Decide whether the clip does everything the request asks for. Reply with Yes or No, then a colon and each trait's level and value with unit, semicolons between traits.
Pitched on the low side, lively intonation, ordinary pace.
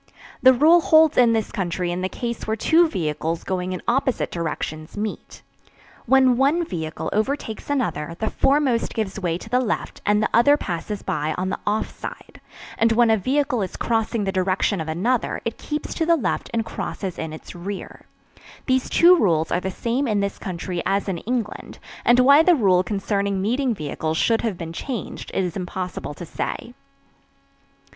No: high, 210 Hz; wide, 5.7 semitones; average, 185 wpm